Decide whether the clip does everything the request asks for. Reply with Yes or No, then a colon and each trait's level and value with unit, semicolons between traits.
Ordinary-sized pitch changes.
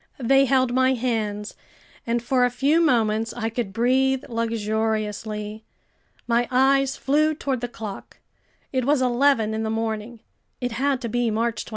Yes: average, 3.0 semitones